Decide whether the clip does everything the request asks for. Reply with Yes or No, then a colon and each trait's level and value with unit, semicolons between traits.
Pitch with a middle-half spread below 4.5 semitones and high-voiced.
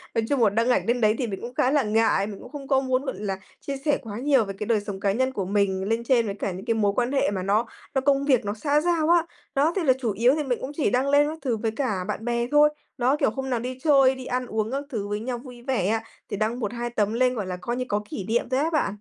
Yes: average, 4.1 semitones; high, 240 Hz